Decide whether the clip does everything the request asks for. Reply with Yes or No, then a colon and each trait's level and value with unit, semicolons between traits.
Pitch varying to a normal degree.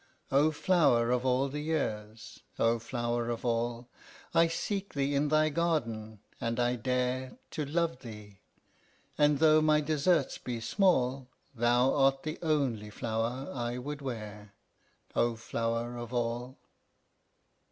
Yes: average, 4.1 semitones